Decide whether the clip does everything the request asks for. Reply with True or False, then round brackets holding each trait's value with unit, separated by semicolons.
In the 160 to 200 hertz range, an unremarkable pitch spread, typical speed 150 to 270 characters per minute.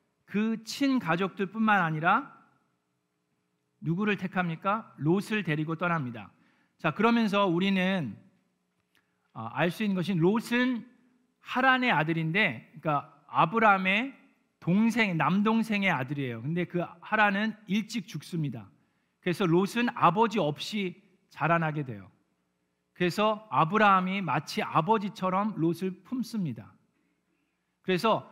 False (185 Hz; 5.7 semitones; 260 characters per minute)